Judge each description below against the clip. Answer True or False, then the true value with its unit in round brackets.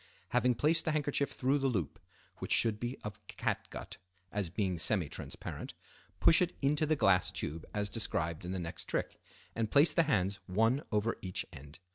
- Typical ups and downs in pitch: False (7.3 semitones)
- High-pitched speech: False (105 Hz)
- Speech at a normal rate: True (180 wpm)